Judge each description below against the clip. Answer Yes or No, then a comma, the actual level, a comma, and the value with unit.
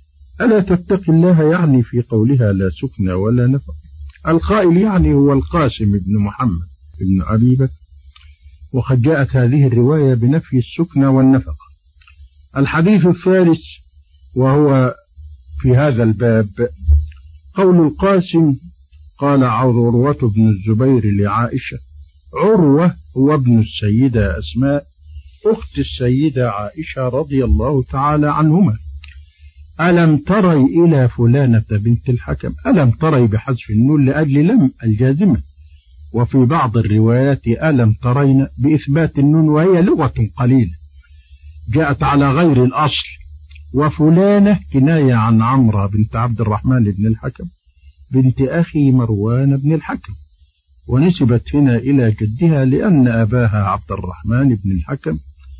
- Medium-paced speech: Yes, average, 110 wpm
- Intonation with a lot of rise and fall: Yes, wide, 6.8 semitones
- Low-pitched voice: Yes, low, 125 Hz